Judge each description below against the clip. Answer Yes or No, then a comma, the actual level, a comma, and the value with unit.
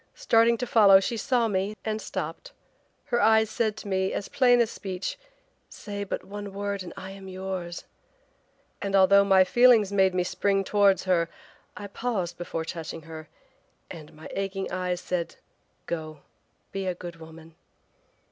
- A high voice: Yes, high, 195 Hz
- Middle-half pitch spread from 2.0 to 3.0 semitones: Yes, average, 2.7 semitones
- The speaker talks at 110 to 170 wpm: Yes, average, 160 wpm